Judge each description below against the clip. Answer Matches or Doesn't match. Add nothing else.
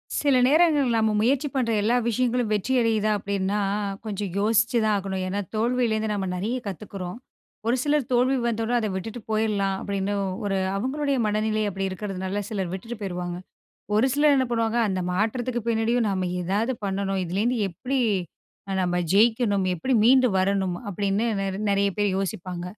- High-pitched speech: Matches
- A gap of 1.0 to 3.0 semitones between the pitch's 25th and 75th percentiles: Doesn't match